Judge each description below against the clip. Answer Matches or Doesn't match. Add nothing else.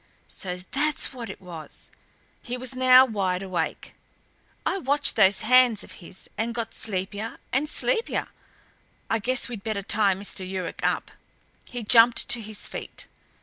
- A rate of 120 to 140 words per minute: Doesn't match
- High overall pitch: Matches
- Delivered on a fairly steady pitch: Doesn't match